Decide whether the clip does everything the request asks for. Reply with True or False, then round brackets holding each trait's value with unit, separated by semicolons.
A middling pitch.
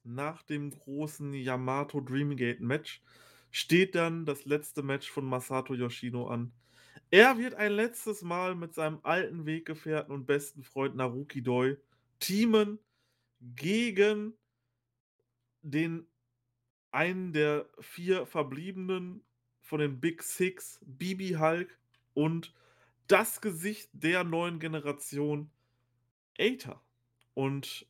True (145 Hz)